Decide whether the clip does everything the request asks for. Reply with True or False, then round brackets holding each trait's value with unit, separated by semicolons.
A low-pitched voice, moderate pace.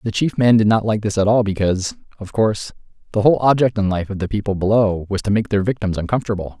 False (105 Hz; 245 wpm)